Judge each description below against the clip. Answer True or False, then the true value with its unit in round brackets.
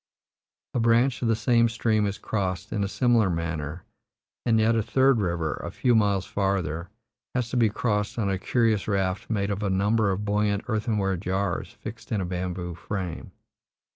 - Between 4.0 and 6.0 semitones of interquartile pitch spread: False (3.3 semitones)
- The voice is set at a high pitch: False (105 Hz)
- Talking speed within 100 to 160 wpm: False (180 wpm)